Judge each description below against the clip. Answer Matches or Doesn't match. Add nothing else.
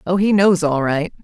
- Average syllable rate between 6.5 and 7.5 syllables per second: Doesn't match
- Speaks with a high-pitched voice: Doesn't match